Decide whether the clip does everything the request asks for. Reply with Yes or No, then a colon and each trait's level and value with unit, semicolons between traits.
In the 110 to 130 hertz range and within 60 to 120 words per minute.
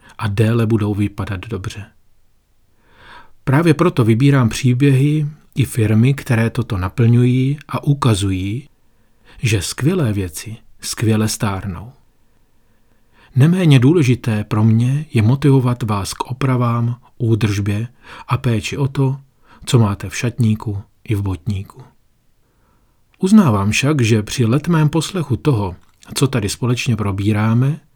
Yes: low, 115 Hz; slow, 115 wpm